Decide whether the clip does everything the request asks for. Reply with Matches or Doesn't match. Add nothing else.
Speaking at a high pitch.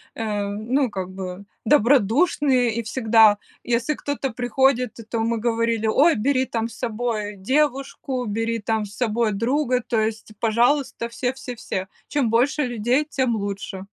Matches